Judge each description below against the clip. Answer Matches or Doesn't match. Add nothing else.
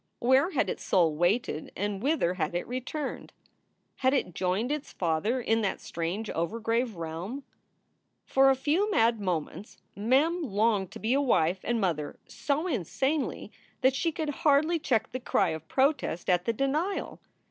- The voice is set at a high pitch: Matches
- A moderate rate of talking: Matches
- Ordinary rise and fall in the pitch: Doesn't match